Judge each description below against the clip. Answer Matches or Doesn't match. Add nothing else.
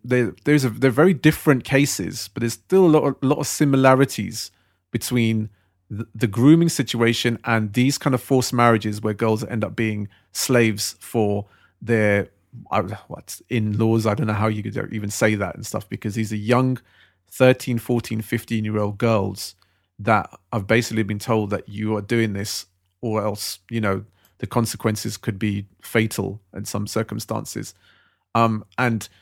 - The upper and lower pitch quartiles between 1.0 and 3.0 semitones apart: Matches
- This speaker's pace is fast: Doesn't match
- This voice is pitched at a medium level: Doesn't match